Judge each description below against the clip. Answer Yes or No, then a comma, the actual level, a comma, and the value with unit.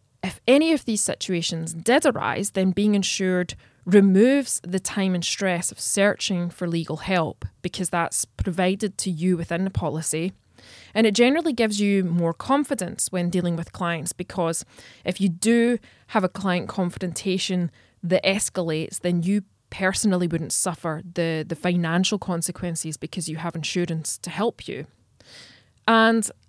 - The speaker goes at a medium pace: Yes, average, 150 wpm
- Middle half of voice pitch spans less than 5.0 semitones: Yes, average, 2.9 semitones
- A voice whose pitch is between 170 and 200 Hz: Yes, medium, 185 Hz